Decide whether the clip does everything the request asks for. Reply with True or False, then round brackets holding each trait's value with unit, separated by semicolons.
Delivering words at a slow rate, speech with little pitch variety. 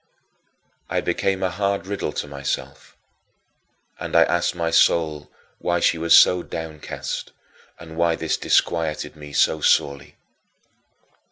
True (125 wpm; 2.2 semitones)